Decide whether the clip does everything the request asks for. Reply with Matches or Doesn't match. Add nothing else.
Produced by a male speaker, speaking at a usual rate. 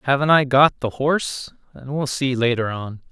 Matches